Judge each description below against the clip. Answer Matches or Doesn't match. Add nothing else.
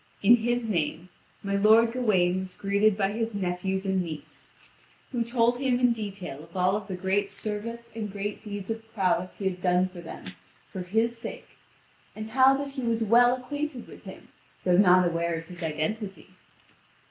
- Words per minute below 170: Doesn't match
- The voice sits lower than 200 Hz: Doesn't match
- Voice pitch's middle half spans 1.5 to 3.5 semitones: Doesn't match